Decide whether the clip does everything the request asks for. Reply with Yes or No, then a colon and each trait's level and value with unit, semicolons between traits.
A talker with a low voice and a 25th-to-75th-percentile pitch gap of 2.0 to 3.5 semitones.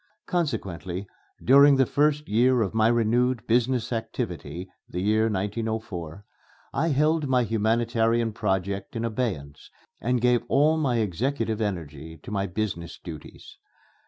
No: low, 110 Hz; average, 4.3 semitones